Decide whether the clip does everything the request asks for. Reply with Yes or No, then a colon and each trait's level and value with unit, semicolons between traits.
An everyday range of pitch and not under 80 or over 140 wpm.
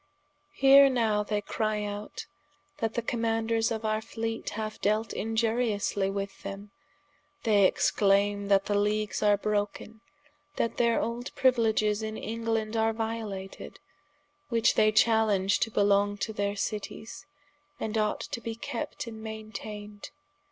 No: narrow, 1.6 semitones; slow, 135 wpm